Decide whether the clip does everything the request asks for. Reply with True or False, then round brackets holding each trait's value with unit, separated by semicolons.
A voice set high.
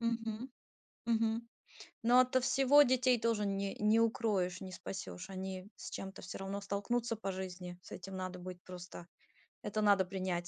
True (200 Hz)